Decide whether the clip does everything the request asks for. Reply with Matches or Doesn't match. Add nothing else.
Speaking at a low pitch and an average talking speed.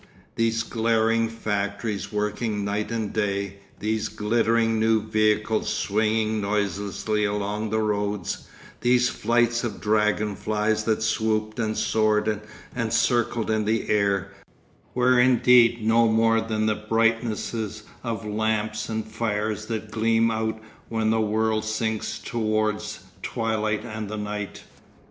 Doesn't match